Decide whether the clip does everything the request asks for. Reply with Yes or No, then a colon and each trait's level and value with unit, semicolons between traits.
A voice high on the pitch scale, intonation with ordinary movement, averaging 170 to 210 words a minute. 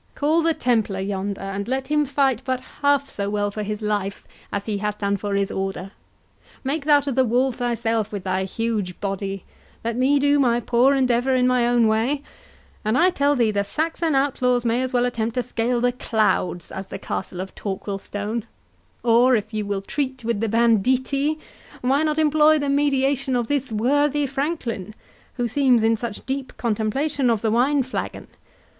Yes: high, 240 Hz; average, 4.5 semitones; average, 180 wpm